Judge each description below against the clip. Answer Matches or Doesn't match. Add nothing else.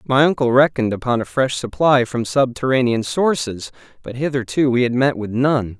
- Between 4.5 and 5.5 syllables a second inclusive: Matches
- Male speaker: Matches